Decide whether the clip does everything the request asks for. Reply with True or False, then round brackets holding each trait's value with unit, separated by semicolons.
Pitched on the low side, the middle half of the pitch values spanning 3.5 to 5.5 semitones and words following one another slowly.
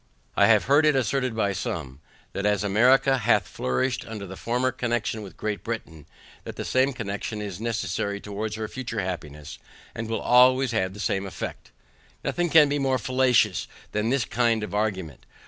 False (110 Hz; 4.3 semitones; 180 wpm)